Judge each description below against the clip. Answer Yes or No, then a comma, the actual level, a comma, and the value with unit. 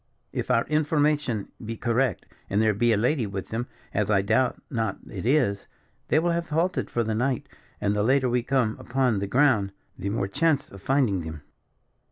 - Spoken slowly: No, average, 195 wpm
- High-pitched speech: No, low, 120 Hz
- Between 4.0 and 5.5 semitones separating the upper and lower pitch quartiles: Yes, average, 5.1 semitones